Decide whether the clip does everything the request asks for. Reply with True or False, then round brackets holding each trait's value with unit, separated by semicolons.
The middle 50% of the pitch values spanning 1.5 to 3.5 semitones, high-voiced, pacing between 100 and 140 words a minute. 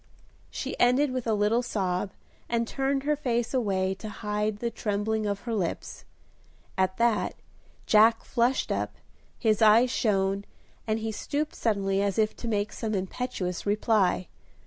False (2.8 semitones; 215 Hz; 150 wpm)